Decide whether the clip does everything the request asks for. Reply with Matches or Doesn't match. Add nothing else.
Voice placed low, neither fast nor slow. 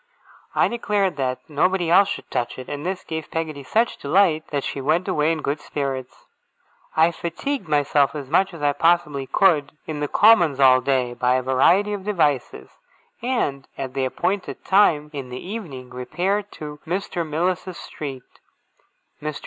Doesn't match